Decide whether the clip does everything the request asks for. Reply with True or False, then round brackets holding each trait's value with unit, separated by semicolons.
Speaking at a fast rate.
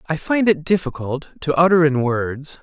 False (185 wpm)